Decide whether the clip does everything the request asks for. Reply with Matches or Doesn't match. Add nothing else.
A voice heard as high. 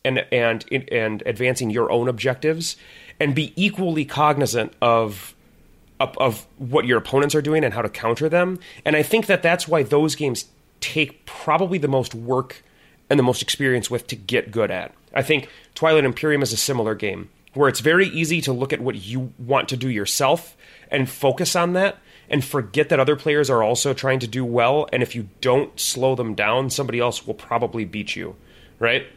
Doesn't match